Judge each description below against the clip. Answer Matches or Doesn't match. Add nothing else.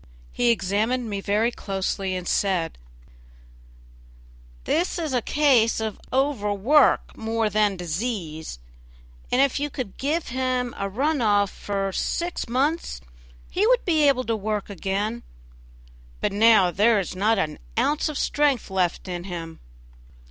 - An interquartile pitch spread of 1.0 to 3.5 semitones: Doesn't match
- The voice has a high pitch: Matches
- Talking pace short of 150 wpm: Matches